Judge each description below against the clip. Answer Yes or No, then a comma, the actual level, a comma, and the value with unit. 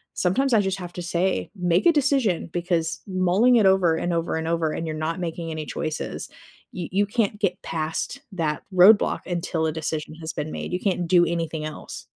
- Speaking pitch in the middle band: Yes, medium, 175 Hz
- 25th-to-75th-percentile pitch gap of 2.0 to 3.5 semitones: Yes, average, 2.9 semitones